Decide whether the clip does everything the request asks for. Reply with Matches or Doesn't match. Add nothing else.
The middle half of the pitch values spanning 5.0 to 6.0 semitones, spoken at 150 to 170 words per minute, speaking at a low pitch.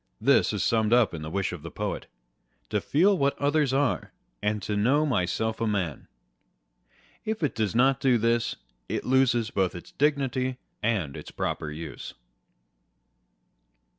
Matches